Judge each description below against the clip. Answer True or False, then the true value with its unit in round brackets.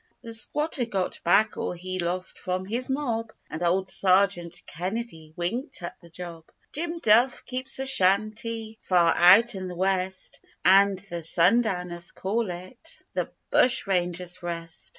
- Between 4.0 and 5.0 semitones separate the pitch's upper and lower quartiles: True (4.5 semitones)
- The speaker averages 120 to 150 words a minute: True (145 wpm)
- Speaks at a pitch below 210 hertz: True (190 Hz)